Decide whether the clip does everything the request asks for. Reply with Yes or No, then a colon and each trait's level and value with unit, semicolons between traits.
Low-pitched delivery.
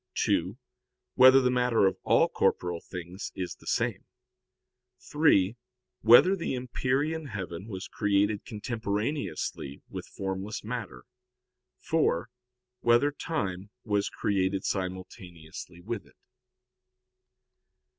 Yes: low, 105 Hz